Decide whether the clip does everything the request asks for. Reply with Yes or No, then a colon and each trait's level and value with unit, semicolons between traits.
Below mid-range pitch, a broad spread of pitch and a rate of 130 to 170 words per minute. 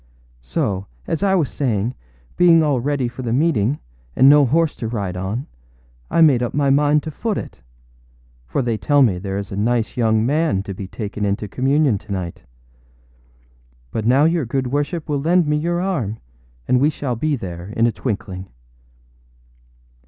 No: low, 125 Hz; wide, 6.0 semitones; average, 180 wpm